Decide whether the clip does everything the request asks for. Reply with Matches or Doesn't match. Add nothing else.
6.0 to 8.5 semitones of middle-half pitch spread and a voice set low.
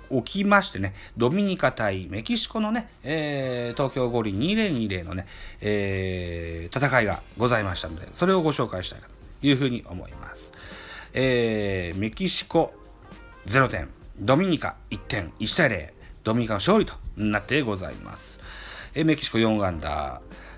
Matches